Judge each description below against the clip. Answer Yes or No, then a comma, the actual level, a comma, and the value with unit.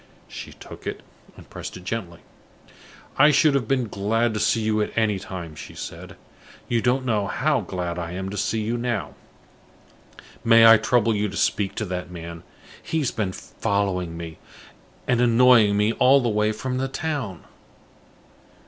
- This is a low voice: Yes, low, 110 Hz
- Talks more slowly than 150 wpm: No, average, 175 wpm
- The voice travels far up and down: No, average, 4.2 semitones